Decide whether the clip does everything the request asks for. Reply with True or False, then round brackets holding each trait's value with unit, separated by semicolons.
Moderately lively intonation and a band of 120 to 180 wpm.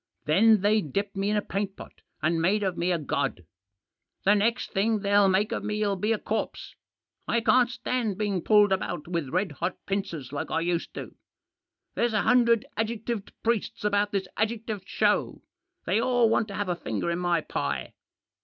False (3.6 semitones; 190 wpm)